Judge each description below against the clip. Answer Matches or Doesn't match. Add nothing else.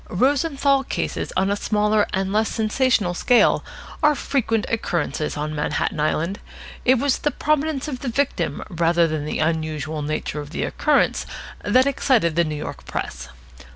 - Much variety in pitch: Matches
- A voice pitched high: Matches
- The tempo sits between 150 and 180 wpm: Matches